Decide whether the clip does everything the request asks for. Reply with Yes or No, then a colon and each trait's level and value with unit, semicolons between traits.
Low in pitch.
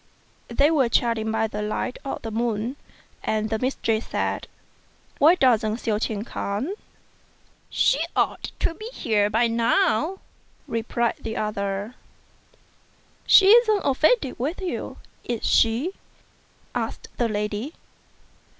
No: high, 230 Hz